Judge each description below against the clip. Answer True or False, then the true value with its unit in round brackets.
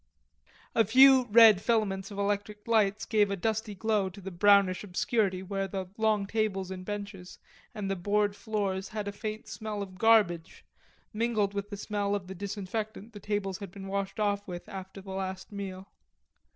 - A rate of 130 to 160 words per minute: False (180 wpm)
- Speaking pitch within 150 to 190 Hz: False (200 Hz)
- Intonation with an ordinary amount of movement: False (1.9 semitones)